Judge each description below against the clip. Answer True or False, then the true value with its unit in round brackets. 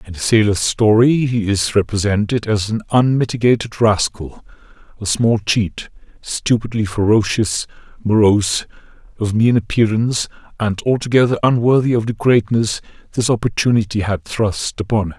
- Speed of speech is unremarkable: False (125 wpm)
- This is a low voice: True (110 Hz)